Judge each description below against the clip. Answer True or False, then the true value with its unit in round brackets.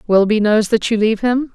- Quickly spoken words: True (235 wpm)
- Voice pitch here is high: True (220 Hz)